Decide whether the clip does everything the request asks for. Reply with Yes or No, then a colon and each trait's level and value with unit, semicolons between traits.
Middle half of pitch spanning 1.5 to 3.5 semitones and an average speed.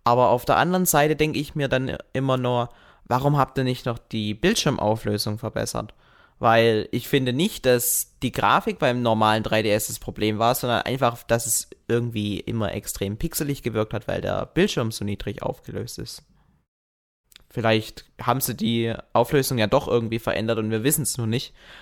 Yes: average, 3.2 semitones; average, 175 wpm